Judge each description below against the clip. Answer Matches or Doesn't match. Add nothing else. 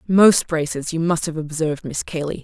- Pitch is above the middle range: Doesn't match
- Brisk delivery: Doesn't match